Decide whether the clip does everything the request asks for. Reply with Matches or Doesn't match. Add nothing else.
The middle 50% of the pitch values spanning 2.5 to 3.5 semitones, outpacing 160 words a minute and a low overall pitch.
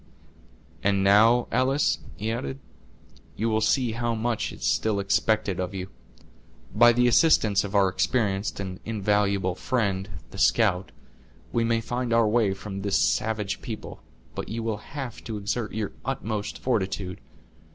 Doesn't match